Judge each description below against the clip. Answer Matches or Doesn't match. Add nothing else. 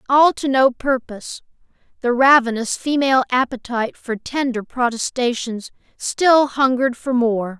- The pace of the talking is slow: Matches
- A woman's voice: Matches